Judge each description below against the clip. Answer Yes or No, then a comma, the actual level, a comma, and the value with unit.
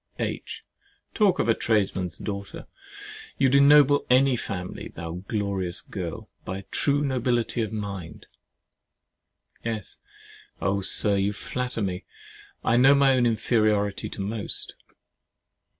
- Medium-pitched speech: No, low, 110 Hz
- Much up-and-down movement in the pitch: No, average, 4.4 semitones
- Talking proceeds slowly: Yes, slow, 120 wpm